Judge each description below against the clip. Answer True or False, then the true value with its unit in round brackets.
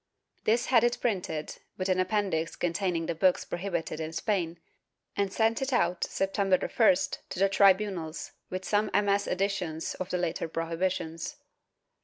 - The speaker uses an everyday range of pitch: True (3.2 semitones)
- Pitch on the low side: False (185 Hz)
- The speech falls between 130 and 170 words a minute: True (145 wpm)